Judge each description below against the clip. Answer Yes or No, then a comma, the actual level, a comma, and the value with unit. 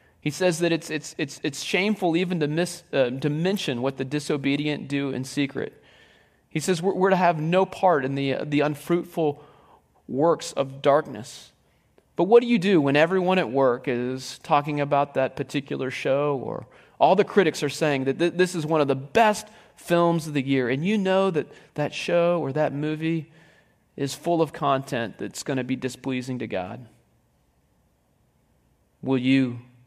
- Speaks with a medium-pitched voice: Yes, medium, 150 Hz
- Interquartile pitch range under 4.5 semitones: Yes, average, 4.1 semitones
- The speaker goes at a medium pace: Yes, average, 185 wpm